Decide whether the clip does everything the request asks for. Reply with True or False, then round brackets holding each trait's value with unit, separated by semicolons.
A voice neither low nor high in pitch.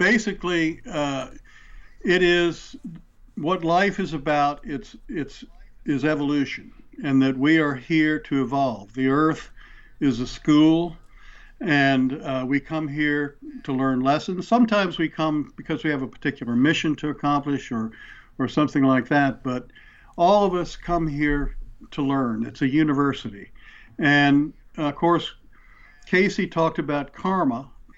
True (150 Hz)